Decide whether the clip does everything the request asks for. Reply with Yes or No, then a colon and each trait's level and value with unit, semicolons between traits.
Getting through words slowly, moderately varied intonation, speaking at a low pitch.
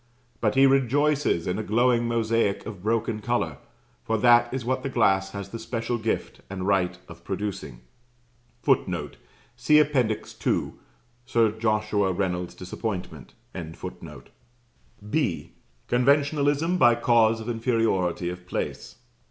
Yes: slow, 125 wpm; average, 4.0 semitones; low, 115 Hz